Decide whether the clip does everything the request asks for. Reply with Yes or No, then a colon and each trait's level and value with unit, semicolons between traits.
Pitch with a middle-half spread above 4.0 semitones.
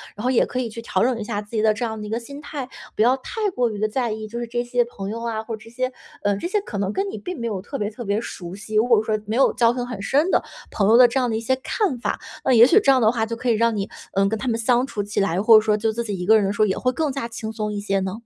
No: average, 2.8 semitones